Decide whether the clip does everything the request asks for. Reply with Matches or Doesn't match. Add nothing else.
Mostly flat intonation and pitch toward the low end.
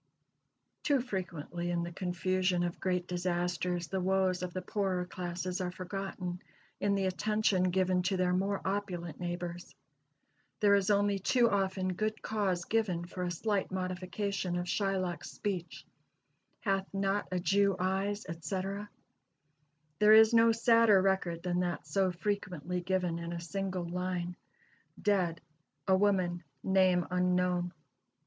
Doesn't match